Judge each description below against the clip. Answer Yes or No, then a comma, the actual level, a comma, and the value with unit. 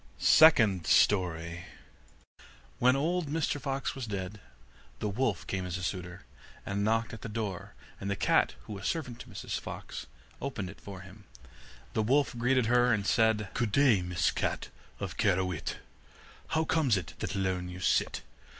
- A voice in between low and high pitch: No, low, 105 Hz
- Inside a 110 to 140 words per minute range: No, average, 165 wpm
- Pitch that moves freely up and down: No, average, 5.0 semitones